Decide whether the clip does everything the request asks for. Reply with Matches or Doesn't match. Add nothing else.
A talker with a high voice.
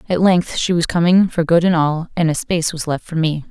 Doesn't match